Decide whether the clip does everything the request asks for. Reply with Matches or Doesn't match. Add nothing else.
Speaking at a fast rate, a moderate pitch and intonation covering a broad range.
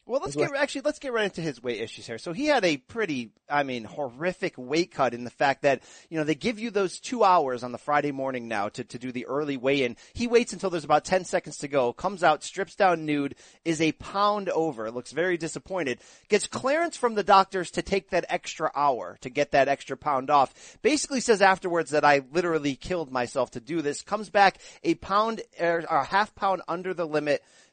Matches